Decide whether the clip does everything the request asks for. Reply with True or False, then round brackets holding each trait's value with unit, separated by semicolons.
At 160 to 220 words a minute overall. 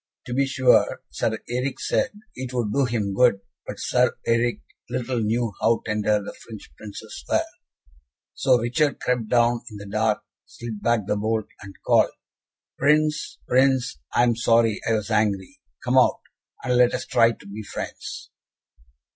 True (165 wpm)